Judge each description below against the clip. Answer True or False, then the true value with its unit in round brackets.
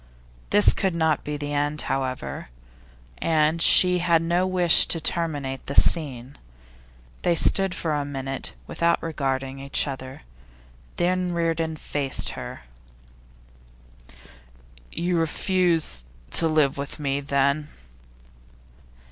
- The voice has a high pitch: False (155 Hz)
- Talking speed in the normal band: False (115 wpm)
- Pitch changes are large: False (3.5 semitones)